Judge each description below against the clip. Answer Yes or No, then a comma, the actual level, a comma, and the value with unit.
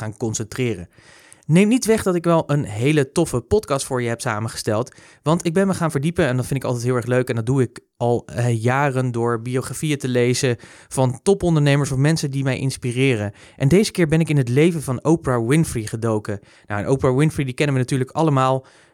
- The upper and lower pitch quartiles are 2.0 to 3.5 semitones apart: No, average, 4.0 semitones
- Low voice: Yes, low, 130 Hz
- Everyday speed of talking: No, fast, 220 wpm